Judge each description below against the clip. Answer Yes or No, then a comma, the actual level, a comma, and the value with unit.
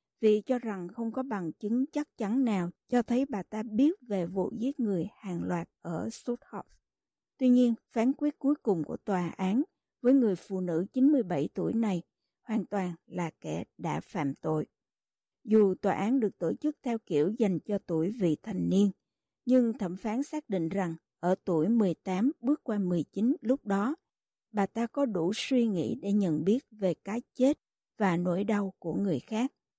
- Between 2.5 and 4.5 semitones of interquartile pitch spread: No, average, 5.3 semitones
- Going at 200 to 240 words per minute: No, average, 185 wpm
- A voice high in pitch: Yes, high, 215 Hz